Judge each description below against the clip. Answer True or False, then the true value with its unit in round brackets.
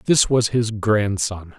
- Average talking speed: True (150 wpm)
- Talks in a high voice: False (110 Hz)